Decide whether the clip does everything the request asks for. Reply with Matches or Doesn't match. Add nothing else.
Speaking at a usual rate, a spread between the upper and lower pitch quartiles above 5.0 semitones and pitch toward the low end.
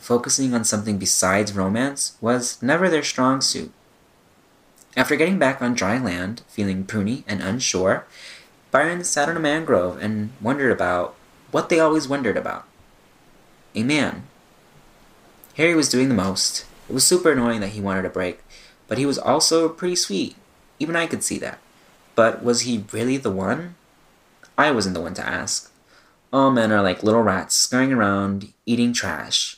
Matches